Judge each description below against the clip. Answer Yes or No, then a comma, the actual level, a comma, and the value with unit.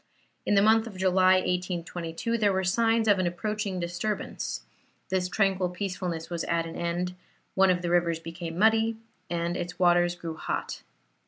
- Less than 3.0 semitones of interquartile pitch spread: Yes, narrow, 2.5 semitones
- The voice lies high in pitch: No, medium, 180 Hz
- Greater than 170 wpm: No, average, 165 wpm